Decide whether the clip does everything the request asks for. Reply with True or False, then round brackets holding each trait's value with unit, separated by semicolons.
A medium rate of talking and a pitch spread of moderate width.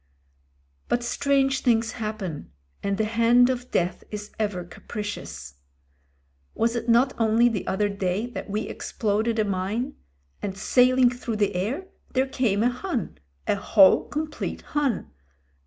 True (145 wpm; 3.6 semitones)